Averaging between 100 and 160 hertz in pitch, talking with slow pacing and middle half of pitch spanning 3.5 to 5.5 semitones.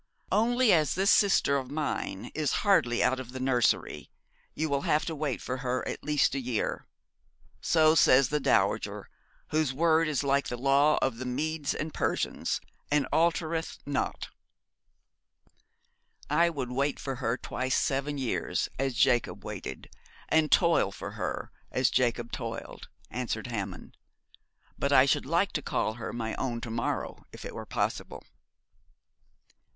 No: low, 135 Hz; average, 155 wpm; average, 3.8 semitones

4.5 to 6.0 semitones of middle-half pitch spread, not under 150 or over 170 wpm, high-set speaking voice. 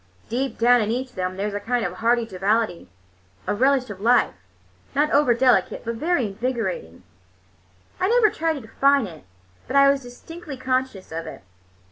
No: average, 4.9 semitones; average, 180 wpm; high, 245 Hz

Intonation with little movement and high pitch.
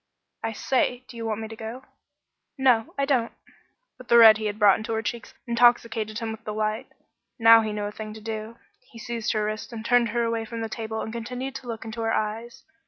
Yes: narrow, 1.4 semitones; high, 225 Hz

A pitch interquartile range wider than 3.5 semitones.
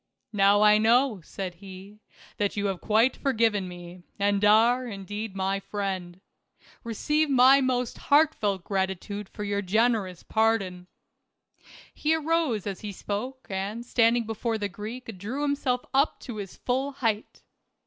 Yes: average, 4.0 semitones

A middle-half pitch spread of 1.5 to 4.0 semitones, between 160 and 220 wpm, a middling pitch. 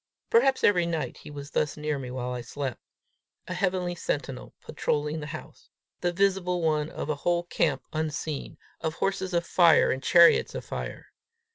Yes: average, 3.4 semitones; average, 170 wpm; medium, 160 Hz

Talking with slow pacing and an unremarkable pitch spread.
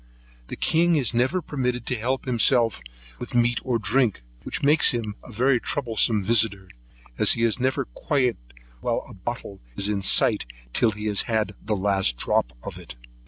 No: average, 175 wpm; average, 3.6 semitones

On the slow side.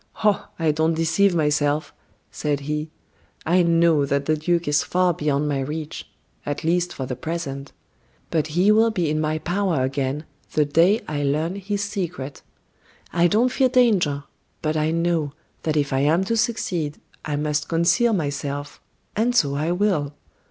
No: average, 165 wpm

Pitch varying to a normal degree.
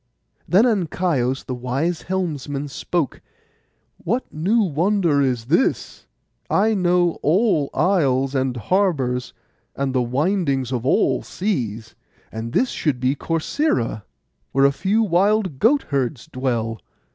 No: wide, 6.6 semitones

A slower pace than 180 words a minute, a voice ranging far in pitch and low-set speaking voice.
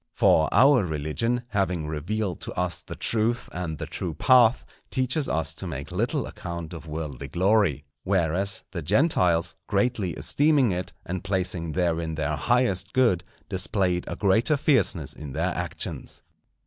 Yes: average, 150 wpm; wide, 5.7 semitones; very low, 90 Hz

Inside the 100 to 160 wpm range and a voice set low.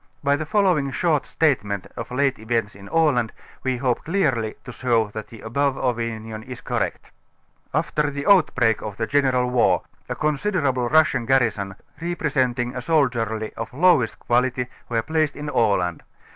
Yes: average, 155 wpm; low, 125 Hz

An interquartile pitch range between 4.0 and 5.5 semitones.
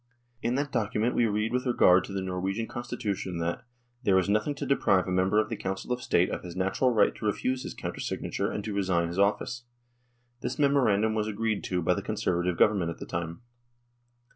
Yes: average, 4.4 semitones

